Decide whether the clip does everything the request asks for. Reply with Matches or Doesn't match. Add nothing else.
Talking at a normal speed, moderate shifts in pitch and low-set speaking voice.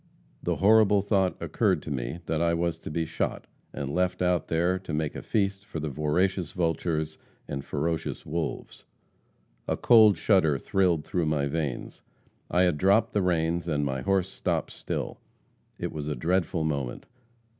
Matches